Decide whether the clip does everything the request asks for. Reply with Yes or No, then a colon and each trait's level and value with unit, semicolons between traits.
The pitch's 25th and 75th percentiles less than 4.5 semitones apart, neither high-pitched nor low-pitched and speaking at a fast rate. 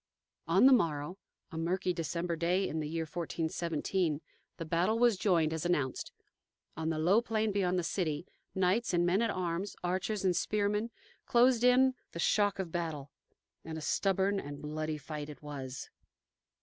No: average, 4.0 semitones; medium, 175 Hz; average, 165 wpm